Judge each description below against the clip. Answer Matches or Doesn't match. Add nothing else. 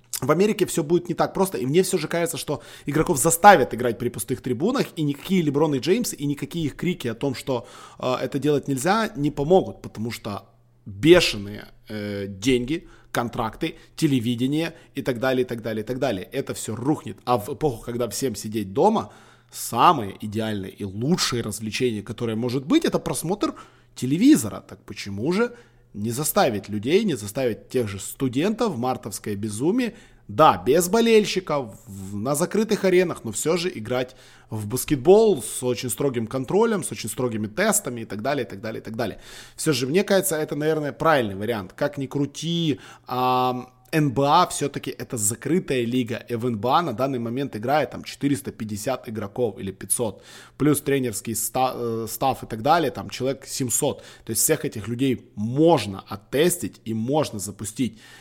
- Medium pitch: Doesn't match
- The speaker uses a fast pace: Matches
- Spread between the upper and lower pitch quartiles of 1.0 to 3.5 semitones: Doesn't match